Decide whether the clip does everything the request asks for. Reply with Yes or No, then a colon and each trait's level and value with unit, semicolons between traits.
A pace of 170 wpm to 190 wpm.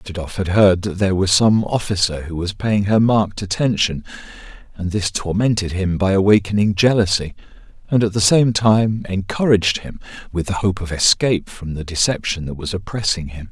Yes: average, 180 wpm